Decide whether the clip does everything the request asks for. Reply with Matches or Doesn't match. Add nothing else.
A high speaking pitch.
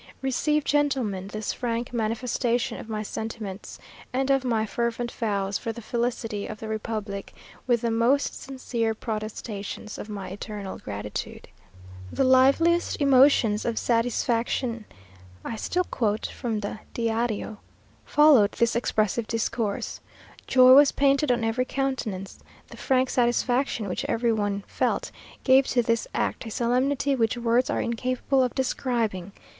Matches